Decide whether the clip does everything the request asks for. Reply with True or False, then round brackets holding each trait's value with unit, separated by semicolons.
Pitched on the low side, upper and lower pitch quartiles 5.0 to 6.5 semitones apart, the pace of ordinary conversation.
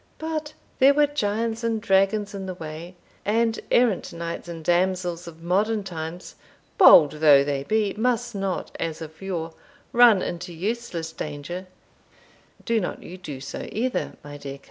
False (185 Hz; 5.4 semitones; 160 wpm)